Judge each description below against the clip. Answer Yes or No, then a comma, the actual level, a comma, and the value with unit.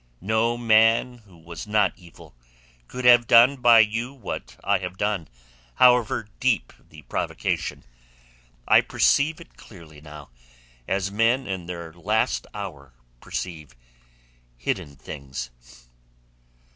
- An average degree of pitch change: No, wide, 7.2 semitones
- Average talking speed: No, slow, 115 wpm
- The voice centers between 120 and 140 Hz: No, low, 100 Hz